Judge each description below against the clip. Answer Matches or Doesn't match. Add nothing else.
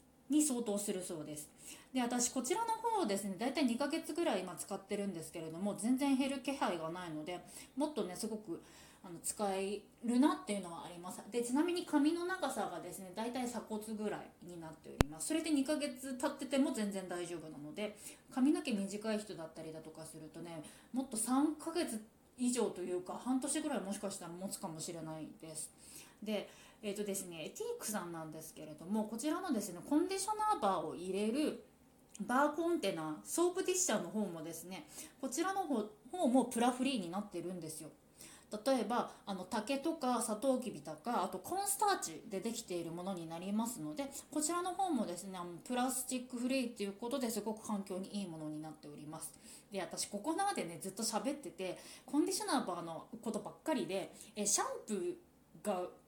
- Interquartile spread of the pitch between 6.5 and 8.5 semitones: Matches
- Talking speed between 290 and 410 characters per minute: Matches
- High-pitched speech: Matches